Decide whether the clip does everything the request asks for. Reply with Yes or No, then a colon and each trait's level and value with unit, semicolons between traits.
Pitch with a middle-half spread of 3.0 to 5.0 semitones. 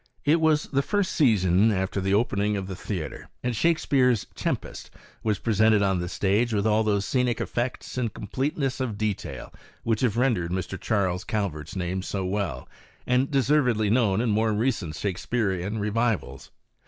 Yes: average, 4.2 semitones